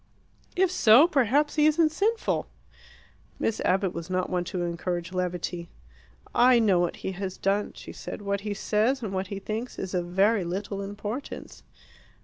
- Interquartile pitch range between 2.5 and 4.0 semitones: No, average, 5.0 semitones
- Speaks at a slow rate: No, average, 165 wpm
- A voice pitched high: Yes, high, 200 Hz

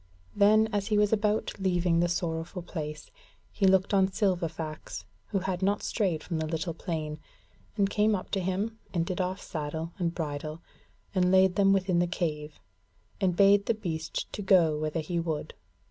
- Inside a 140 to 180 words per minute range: Yes, average, 175 wpm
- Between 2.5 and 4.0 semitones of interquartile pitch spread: Yes, average, 3.3 semitones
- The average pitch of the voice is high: No, medium, 180 Hz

